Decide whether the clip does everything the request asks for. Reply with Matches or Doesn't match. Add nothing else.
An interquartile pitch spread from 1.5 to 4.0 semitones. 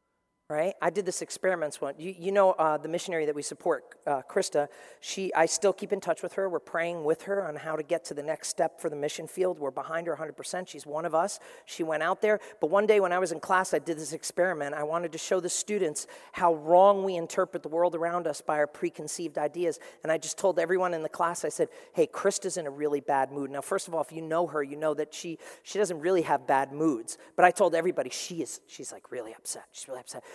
Matches